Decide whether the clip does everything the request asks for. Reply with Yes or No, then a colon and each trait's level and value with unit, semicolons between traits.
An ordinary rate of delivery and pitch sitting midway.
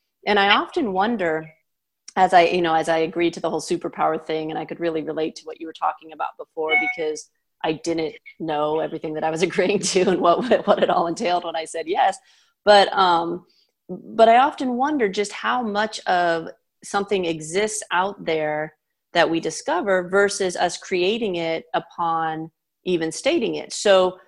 Yes: average, 185 wpm; medium, 175 Hz